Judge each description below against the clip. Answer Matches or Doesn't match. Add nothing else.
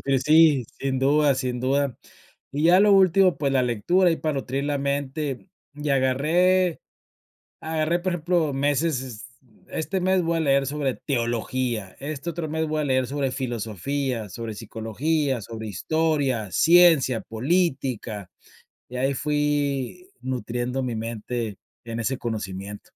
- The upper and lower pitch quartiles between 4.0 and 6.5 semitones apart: Matches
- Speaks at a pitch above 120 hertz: Matches